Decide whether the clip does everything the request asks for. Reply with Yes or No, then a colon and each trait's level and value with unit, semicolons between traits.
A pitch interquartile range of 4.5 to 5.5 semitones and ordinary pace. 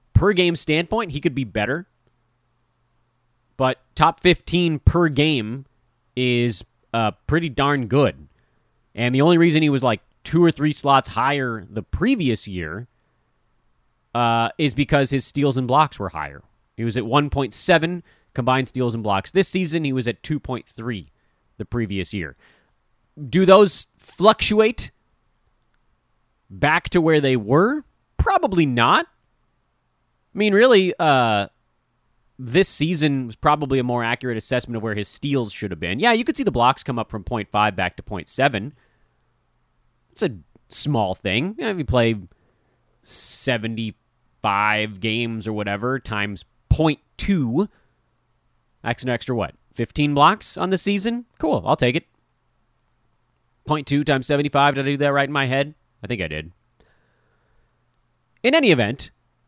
Yes: average, 5.0 semitones; average, 145 wpm